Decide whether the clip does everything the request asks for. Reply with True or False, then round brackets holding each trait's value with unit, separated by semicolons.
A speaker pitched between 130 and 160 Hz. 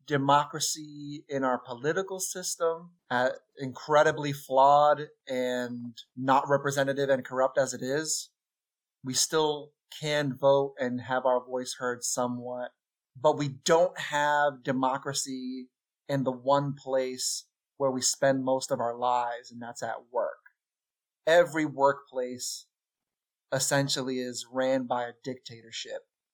True (135 Hz)